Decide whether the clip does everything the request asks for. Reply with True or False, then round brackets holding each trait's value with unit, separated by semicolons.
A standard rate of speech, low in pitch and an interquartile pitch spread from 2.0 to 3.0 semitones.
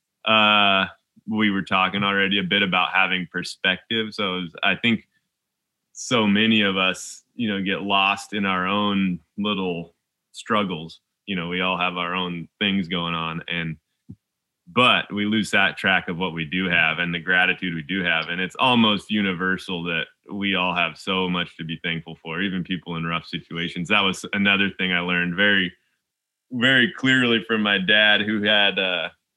True (180 wpm; 95 Hz; 2.6 semitones)